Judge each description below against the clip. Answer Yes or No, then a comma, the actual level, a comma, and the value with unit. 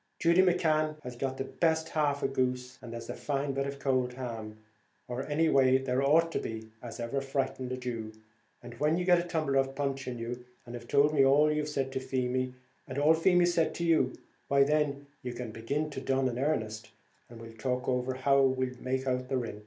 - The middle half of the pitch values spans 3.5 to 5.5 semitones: No, average, 2.9 semitones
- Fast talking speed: Yes, fast, 230 wpm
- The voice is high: No, low, 135 Hz